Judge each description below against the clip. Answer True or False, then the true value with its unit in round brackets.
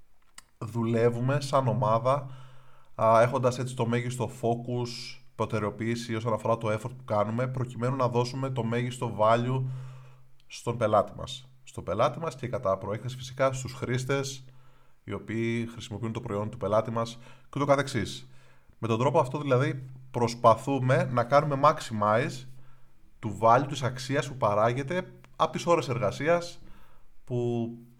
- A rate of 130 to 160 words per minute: True (140 wpm)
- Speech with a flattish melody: True (2.3 semitones)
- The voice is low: True (125 Hz)